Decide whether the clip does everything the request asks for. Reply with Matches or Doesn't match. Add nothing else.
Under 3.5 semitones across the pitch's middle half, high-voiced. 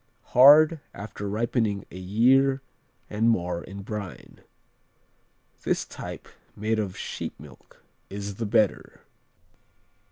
Doesn't match